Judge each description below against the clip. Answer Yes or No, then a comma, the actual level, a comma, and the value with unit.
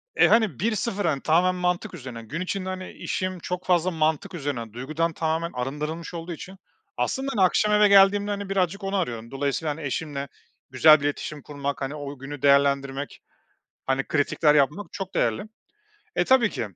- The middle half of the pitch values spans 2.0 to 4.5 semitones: No, average, 5.0 semitones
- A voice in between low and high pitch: Yes, medium, 160 Hz